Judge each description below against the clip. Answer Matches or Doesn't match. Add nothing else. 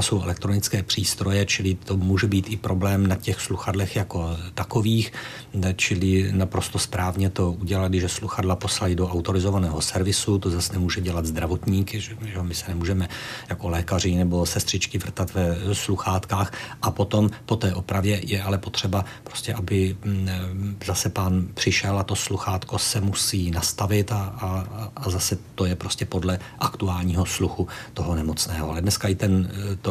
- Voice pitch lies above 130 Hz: Doesn't match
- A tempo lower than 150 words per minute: Doesn't match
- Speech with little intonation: Matches